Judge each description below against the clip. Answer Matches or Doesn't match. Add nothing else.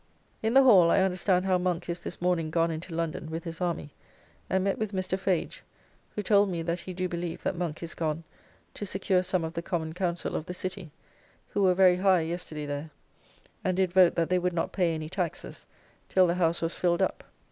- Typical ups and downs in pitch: Doesn't match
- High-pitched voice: Doesn't match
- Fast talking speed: Matches